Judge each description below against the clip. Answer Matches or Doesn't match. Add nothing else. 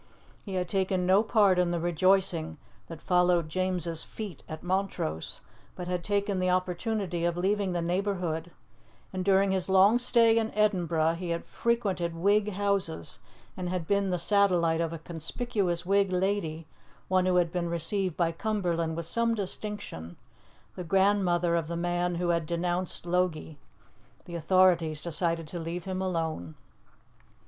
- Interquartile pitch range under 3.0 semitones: Matches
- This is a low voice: Doesn't match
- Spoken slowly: Doesn't match